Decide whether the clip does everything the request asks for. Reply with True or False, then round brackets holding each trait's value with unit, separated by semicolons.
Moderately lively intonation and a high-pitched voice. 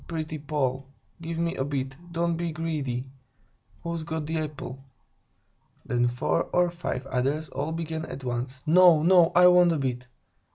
False (4.0 semitones; 155 Hz)